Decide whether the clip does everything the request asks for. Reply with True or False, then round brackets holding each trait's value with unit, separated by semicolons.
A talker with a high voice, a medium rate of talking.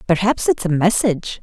True (195 Hz; 170 wpm)